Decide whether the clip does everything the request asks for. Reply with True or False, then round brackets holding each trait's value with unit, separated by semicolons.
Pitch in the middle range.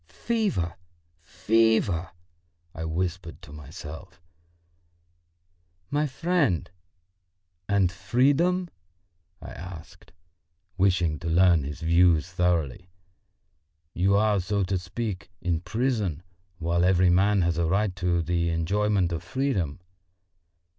False (90 Hz)